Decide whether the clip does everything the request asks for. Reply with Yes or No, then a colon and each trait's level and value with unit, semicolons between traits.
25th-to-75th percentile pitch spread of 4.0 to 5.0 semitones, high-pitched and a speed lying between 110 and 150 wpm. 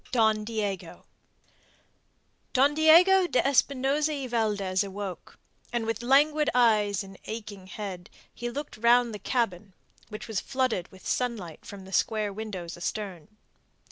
Yes: average, 4.4 semitones; high, 220 Hz; slow, 135 wpm